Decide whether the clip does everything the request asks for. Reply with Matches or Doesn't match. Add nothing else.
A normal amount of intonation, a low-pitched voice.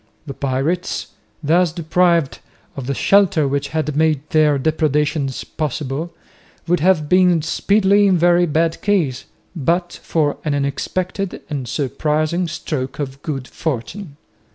Doesn't match